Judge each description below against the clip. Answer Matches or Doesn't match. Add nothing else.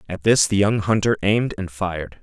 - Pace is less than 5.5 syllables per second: Doesn't match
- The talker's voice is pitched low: Matches